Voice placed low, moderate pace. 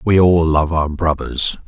Yes: very low, 85 Hz; average, 180 wpm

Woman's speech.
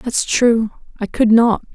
Yes: female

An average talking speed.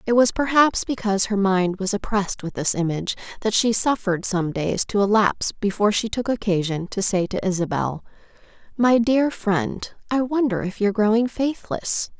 Yes: average, 170 wpm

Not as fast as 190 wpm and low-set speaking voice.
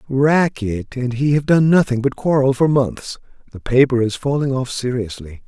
Yes: average, 175 wpm; low, 130 Hz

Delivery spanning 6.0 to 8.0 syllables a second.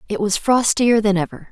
No: 5.3 syllables/s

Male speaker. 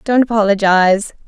No: female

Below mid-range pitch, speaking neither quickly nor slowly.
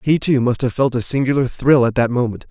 No: low, 130 Hz; fast, 265 wpm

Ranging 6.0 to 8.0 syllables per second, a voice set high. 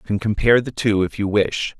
No: 6.2 syllables/s; low, 105 Hz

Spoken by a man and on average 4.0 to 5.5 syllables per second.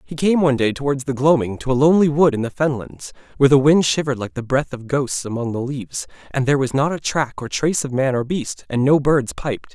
No: male; 6.1 syllables/s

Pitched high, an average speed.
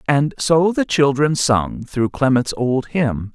No: low, 135 Hz; average, 160 wpm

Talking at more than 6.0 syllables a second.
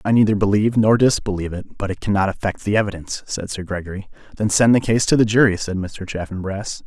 Yes: 6.4 syllables/s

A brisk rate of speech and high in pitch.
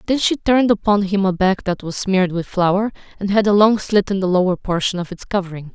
Yes: fast, 250 wpm; high, 195 Hz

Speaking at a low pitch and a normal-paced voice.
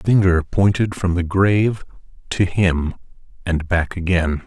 Yes: very low, 90 Hz; average, 150 wpm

